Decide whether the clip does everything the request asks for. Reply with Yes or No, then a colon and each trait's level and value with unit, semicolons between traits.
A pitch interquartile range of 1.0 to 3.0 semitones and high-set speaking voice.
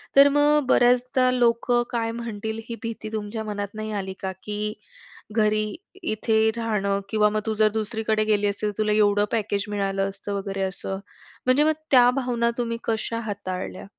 Yes: narrow, 2.4 semitones; high, 215 Hz